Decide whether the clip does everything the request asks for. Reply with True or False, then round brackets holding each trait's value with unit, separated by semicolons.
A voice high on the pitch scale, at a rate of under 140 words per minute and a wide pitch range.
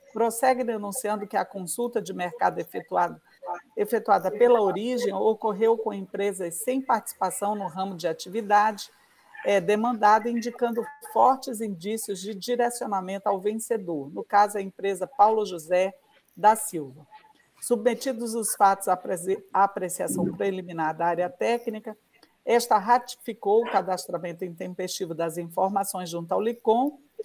False (210 Hz; 125 wpm; 3.8 semitones)